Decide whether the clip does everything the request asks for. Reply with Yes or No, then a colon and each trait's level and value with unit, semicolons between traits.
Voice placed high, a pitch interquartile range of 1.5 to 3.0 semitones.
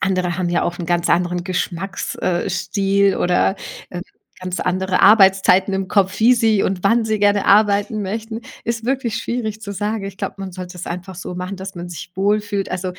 Yes: high, 195 Hz; narrow, 2.5 semitones